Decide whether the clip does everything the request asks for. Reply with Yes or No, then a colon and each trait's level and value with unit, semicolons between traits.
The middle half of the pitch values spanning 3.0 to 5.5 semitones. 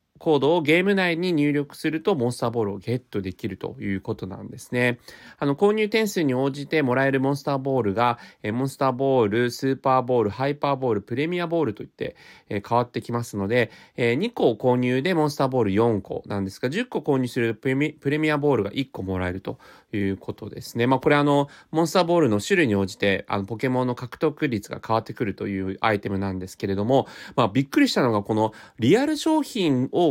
Yes: average, 5.2 semitones